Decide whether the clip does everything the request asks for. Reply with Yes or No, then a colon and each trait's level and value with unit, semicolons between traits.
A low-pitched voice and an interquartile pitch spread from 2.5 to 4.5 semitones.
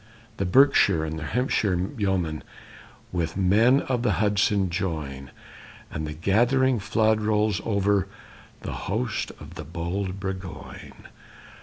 Yes: low, 100 Hz; average, 4.0 semitones